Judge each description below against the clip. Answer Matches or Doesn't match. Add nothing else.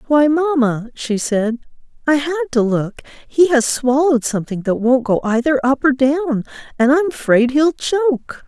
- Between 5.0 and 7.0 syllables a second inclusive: Doesn't match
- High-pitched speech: Matches